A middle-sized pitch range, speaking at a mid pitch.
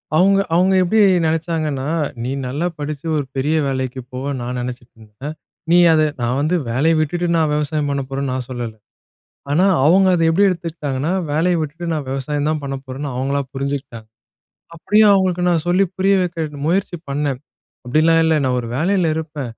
Yes: average, 4.1 semitones; medium, 150 Hz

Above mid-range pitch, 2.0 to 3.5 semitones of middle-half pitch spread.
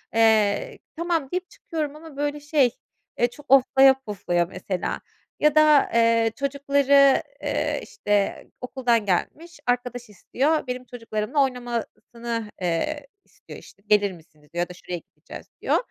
No: high, 245 Hz; average, 5.2 semitones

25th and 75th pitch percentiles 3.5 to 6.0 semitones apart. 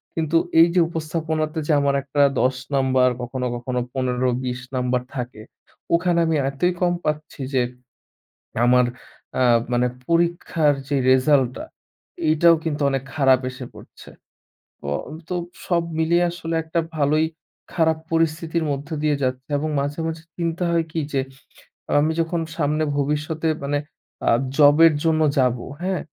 Yes: average, 3.8 semitones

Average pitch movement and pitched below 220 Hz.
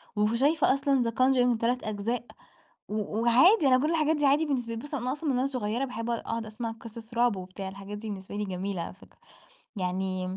No: average, 4.2 semitones; high, 230 Hz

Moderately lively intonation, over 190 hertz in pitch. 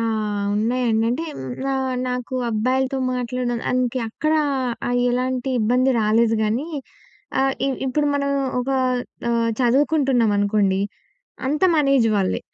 Yes: average, 3.2 semitones; high, 245 Hz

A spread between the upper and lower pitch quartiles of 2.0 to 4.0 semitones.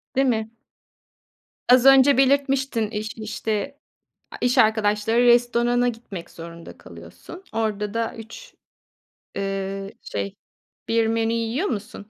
Yes: average, 3.0 semitones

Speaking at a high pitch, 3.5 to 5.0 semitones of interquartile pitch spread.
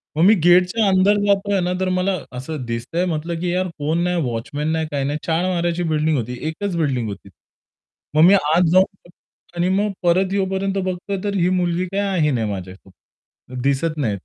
No: medium, 175 Hz; average, 4.2 semitones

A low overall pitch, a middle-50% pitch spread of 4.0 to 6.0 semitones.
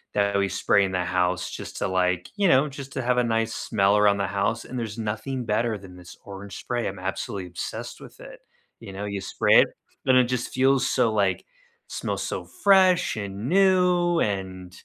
Yes: low, 105 Hz; average, 4.8 semitones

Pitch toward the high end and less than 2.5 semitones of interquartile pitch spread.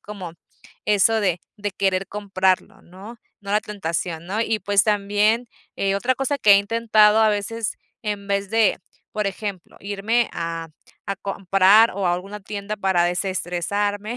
Yes: high, 200 Hz; narrow, 1.9 semitones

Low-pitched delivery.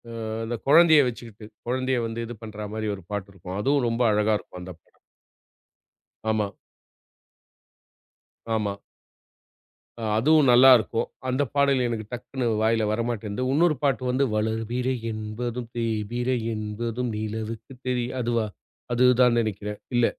Yes: low, 115 Hz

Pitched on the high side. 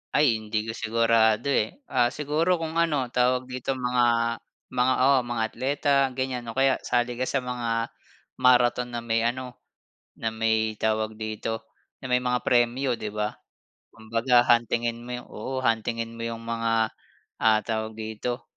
No: low, 120 Hz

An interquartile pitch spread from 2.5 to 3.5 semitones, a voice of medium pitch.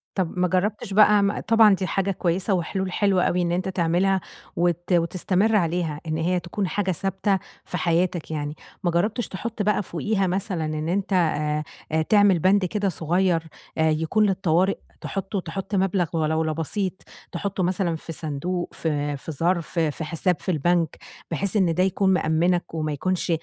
Yes: average, 2.9 semitones; medium, 180 Hz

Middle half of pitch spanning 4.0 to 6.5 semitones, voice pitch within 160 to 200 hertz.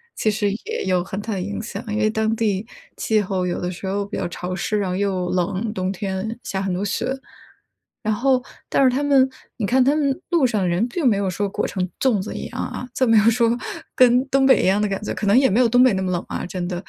No: average, 4.3 semitones; high, 210 Hz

